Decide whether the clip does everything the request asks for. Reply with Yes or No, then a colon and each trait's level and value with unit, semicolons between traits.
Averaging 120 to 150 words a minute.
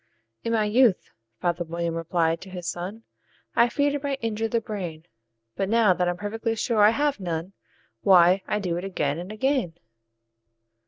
No: average, 175 wpm